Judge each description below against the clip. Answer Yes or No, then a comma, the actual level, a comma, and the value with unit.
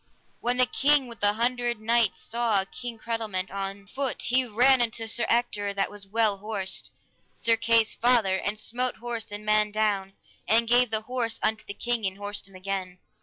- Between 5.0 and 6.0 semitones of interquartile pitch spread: No, average, 2.8 semitones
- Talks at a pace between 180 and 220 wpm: Yes, average, 185 wpm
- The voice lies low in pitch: No, high, 220 Hz